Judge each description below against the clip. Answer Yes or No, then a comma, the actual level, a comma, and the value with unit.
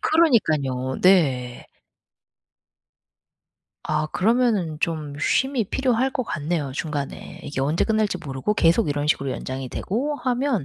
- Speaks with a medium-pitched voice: Yes, medium, 165 Hz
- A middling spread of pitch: No, wide, 8.5 semitones